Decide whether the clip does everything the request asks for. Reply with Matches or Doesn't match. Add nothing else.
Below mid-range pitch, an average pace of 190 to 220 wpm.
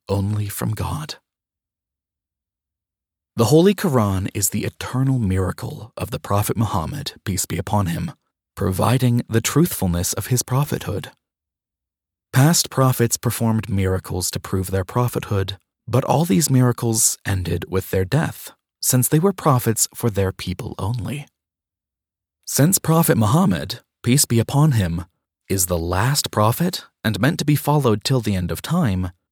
Doesn't match